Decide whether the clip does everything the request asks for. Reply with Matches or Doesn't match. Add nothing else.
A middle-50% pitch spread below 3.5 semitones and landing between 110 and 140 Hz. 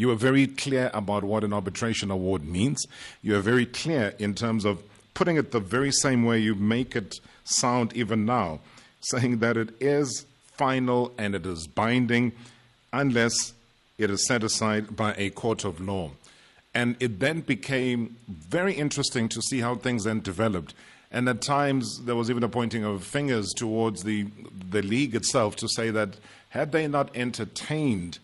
Matches